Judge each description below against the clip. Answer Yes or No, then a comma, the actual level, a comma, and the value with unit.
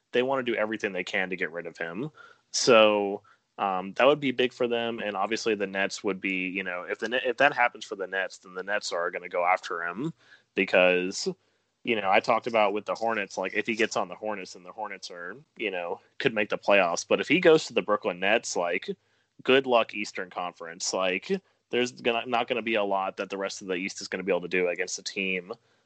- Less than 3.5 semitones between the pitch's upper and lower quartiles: No, average, 4.2 semitones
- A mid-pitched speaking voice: No, low, 105 Hz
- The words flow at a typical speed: No, fast, 255 wpm